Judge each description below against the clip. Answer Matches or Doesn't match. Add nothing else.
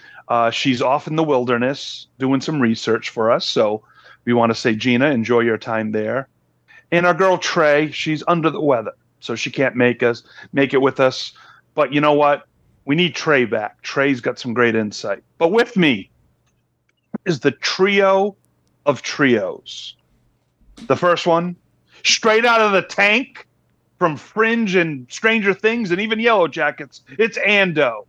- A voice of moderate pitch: Matches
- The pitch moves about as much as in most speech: Doesn't match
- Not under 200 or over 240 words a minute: Doesn't match